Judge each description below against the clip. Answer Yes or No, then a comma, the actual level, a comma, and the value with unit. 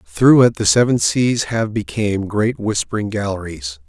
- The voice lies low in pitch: Yes, low, 110 Hz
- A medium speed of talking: Yes, average, 155 wpm